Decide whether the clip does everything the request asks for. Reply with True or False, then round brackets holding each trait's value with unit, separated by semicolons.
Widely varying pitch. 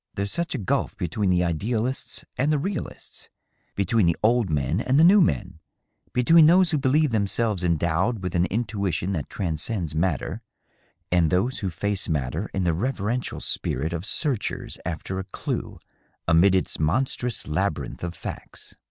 True (6.4 semitones)